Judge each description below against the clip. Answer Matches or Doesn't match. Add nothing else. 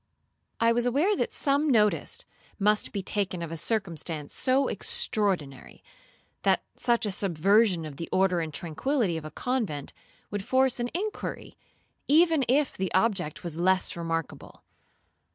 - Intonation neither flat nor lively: Doesn't match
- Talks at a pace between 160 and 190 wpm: Doesn't match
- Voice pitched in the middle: Doesn't match